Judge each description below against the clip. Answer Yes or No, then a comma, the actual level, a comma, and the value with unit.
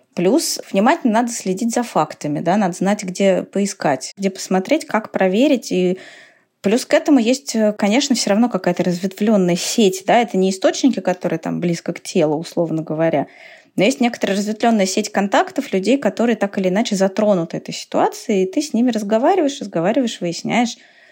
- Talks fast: Yes, fast, 170 wpm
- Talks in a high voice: Yes, high, 210 Hz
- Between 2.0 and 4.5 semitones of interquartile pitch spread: No, average, 4.9 semitones